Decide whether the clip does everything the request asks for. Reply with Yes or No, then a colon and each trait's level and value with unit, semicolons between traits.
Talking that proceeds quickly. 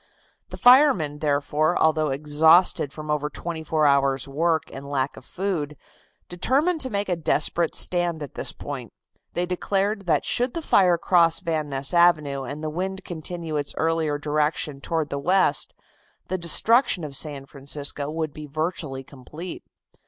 No: average, 160 wpm